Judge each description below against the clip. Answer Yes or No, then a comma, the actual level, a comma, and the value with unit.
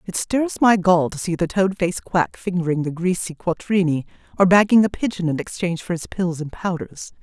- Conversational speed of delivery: No, fast, 210 wpm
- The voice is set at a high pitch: No, medium, 180 Hz